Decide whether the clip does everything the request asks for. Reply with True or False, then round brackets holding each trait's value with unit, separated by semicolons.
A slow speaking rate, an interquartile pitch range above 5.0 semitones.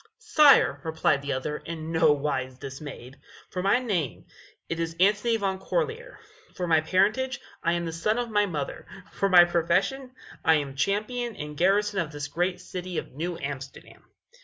False (170 wpm; 5.6 semitones)